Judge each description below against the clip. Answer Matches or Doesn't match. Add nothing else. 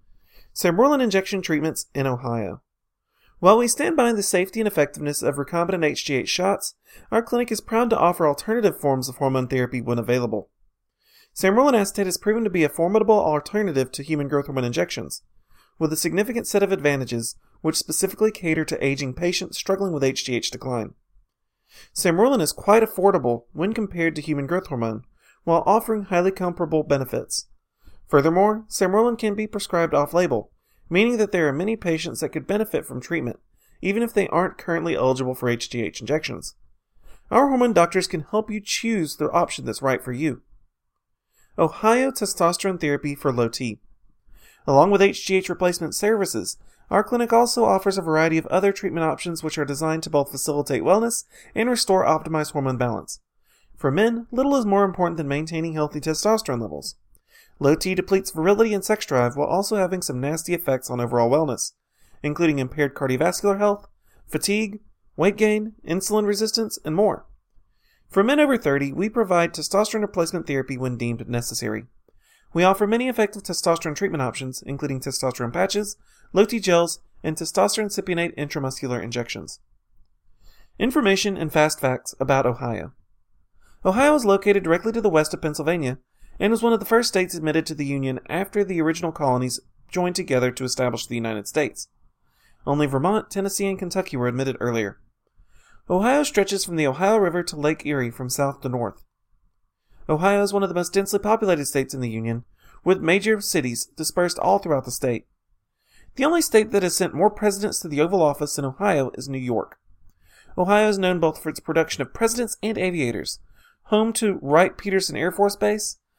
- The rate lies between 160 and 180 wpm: Matches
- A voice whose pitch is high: Doesn't match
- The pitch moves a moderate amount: Doesn't match